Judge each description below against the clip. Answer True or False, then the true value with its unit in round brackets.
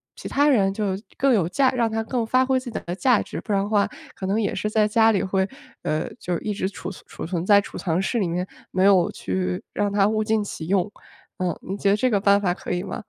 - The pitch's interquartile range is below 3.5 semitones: True (3.0 semitones)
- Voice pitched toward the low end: False (200 Hz)